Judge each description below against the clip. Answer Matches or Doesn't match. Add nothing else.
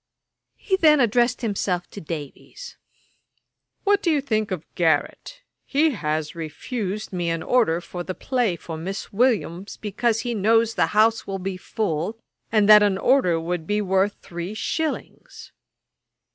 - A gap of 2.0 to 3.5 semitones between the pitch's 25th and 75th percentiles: Doesn't match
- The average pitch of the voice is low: Doesn't match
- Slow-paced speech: Doesn't match